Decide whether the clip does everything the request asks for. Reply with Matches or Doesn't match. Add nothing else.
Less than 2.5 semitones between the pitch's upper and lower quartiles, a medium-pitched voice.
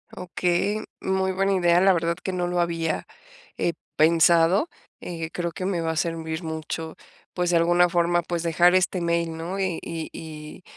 Matches